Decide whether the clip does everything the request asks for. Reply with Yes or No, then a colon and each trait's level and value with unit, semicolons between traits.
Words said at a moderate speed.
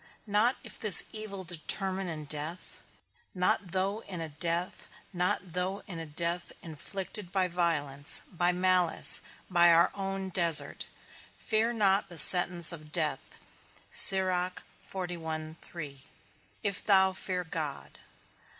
No: slow, 115 wpm